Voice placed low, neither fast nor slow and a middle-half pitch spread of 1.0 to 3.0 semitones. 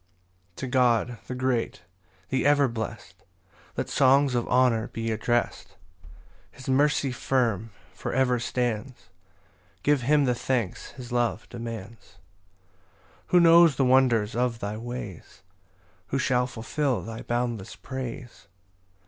No: low, 125 Hz; slow, 130 wpm; narrow, 2.4 semitones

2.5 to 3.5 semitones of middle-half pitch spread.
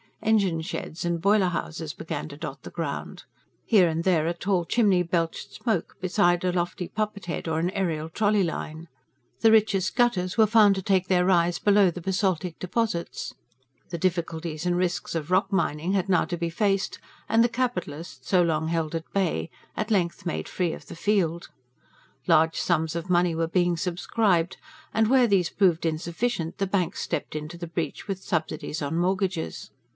Yes: average, 2.9 semitones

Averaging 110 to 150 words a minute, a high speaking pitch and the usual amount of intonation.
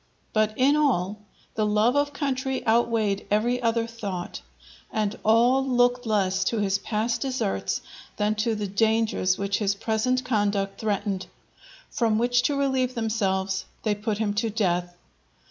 Yes: average, 145 wpm; high, 220 Hz; average, 3.2 semitones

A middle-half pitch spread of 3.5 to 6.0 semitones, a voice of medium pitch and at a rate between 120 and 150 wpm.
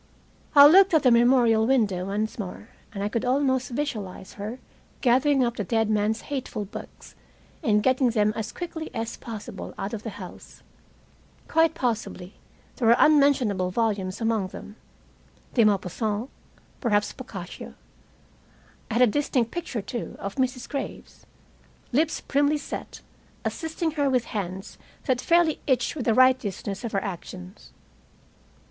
No: average, 4.4 semitones; high, 235 Hz; average, 145 wpm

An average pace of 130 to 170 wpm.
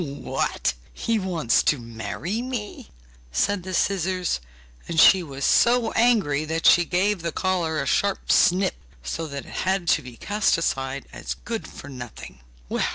Yes: average, 160 wpm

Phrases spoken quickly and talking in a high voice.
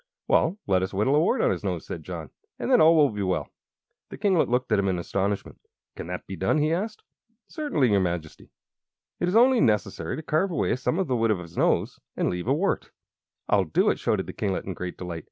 No: fast, 235 wpm; low, 110 Hz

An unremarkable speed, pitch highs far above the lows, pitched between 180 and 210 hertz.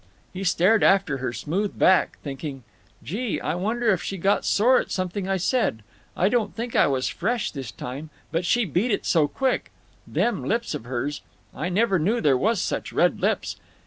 Yes: average, 185 wpm; wide, 7.0 semitones; medium, 185 Hz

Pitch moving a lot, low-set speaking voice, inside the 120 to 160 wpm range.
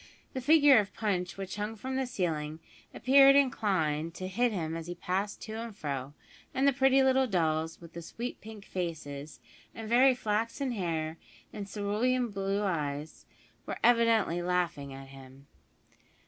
No: wide, 6.5 semitones; high, 195 Hz; average, 155 wpm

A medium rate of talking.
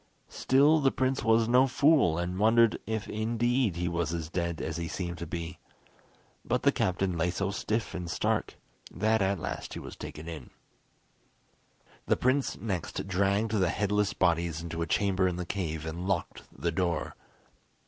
Yes: average, 170 wpm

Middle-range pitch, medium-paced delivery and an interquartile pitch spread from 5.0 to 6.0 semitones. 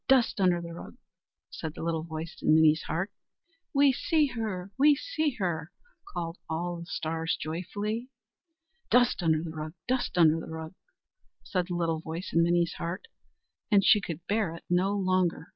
No: medium, 175 Hz; average, 170 wpm; average, 4.2 semitones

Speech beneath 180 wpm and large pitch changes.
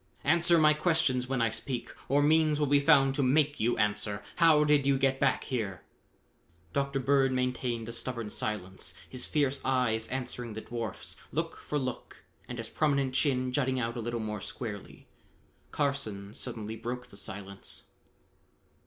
No: average, 160 wpm; average, 3.7 semitones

